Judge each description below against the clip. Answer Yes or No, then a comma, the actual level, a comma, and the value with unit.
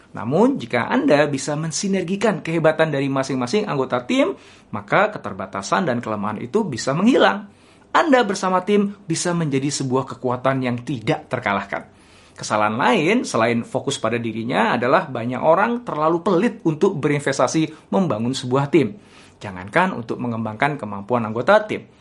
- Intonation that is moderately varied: No, wide, 5.9 semitones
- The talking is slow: No, average, 135 wpm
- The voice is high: No, medium, 140 Hz